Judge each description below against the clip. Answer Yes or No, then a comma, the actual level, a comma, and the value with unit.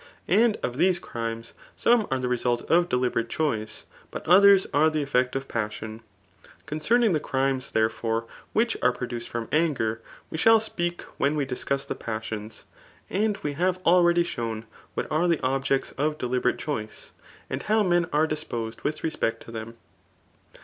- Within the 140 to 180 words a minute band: Yes, average, 165 wpm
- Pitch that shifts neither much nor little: No, wide, 6.7 semitones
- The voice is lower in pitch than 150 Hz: Yes, low, 135 Hz